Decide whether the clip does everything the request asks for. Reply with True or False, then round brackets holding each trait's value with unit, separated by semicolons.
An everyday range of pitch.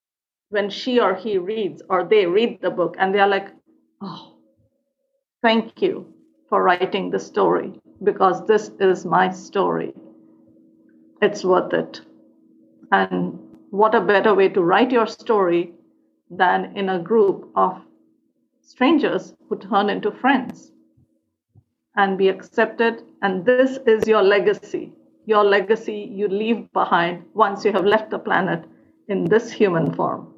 True (3.4 semitones)